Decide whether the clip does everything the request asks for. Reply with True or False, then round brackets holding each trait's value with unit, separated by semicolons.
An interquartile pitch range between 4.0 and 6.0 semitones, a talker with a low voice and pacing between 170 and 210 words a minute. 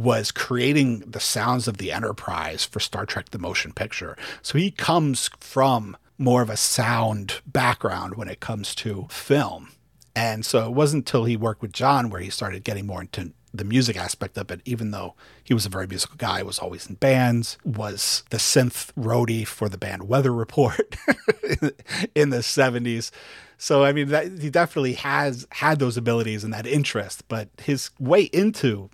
True (4.4 semitones; 120 Hz; 185 wpm)